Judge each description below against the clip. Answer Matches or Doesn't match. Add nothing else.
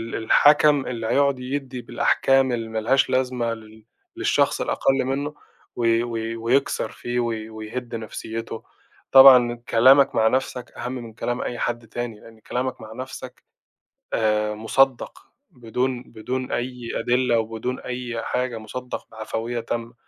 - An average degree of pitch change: Doesn't match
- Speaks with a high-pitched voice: Doesn't match